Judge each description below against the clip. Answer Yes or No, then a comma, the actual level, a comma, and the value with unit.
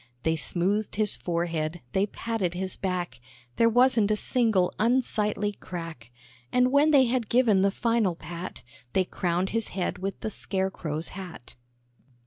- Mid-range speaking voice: No, high, 195 Hz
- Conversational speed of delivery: Yes, average, 150 wpm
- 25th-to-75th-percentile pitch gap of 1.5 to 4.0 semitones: No, average, 4.5 semitones